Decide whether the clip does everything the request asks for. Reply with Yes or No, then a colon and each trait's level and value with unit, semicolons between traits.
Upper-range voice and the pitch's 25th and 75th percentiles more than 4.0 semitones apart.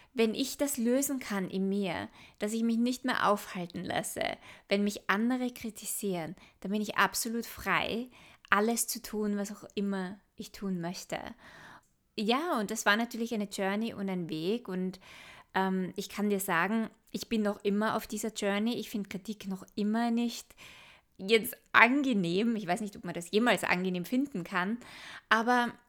No: high, 210 Hz; average, 2.9 semitones